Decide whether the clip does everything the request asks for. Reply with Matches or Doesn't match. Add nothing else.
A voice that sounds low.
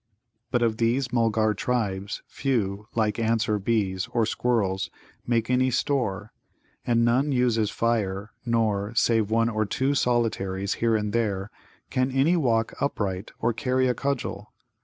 Matches